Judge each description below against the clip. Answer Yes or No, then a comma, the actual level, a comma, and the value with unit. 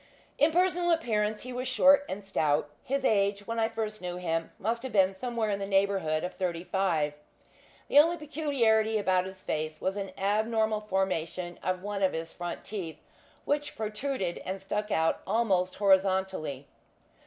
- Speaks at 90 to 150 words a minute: No, average, 165 wpm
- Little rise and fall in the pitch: No, average, 3.7 semitones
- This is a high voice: Yes, high, 200 Hz